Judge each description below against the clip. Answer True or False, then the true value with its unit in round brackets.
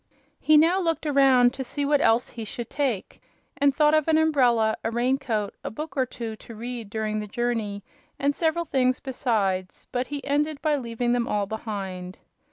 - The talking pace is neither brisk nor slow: True (190 wpm)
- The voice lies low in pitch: False (245 Hz)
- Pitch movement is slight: False (4.7 semitones)